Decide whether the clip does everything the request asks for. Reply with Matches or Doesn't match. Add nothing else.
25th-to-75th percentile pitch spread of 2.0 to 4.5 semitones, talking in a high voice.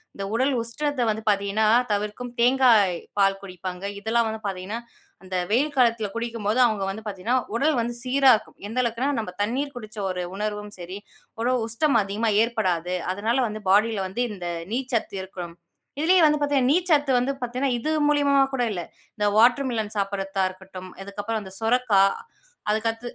Matches